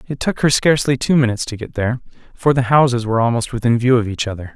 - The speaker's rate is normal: No, fast, 250 wpm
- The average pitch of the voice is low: Yes, low, 120 Hz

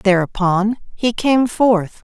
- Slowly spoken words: Yes, slow, 110 wpm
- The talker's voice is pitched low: No, high, 210 Hz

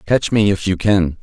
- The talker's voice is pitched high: No, very low, 95 Hz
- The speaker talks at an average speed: No, fast, 245 wpm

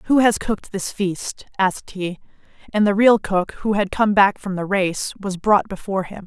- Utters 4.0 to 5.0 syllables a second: Yes, 4.8 syllables/s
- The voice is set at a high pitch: Yes, high, 195 Hz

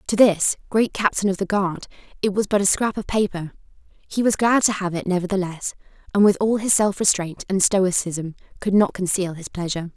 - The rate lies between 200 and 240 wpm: Yes, fast, 205 wpm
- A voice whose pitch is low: No, high, 195 Hz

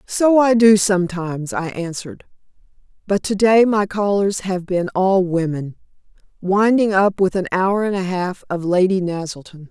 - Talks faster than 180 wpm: No, average, 160 wpm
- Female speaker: Yes, female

